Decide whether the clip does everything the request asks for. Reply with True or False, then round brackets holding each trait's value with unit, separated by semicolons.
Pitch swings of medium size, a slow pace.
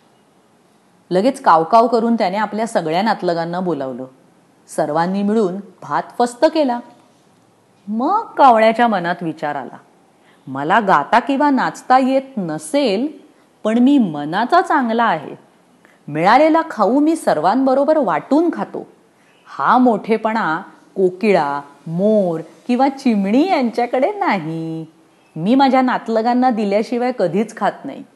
False (6.9 semitones; 105 wpm)